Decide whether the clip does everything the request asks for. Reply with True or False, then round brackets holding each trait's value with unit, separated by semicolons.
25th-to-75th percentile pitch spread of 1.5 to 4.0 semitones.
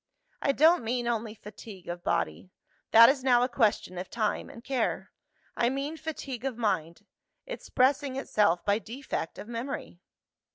False (4.4 semitones)